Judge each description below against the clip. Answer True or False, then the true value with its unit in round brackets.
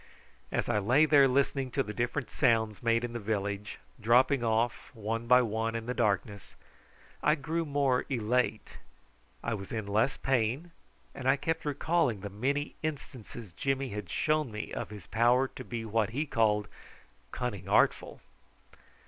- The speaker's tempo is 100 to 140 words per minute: False (160 wpm)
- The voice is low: True (120 Hz)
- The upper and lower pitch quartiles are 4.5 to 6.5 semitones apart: False (4.1 semitones)